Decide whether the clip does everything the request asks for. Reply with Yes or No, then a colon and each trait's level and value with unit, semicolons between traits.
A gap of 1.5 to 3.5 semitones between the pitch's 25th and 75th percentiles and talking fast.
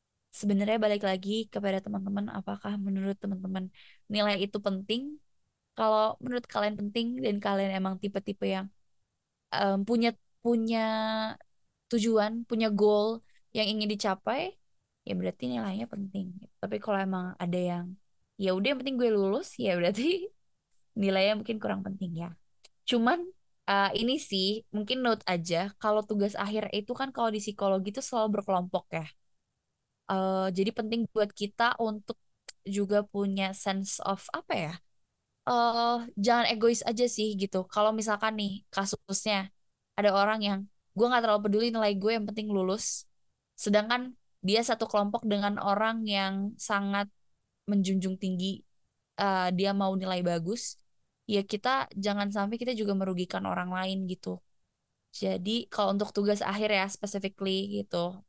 Yes: narrow, 2.4 semitones; fast, 145 wpm